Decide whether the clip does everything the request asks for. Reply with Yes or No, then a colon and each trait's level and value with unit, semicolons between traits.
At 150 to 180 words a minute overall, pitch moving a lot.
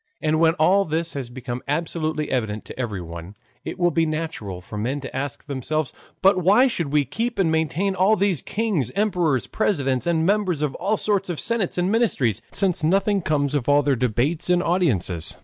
No: average, 190 wpm; wide, 6.1 semitones